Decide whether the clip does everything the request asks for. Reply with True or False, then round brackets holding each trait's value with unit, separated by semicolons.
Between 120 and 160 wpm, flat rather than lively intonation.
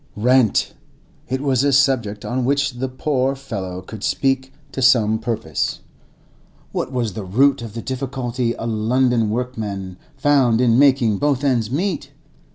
False (145 wpm; 3.2 semitones)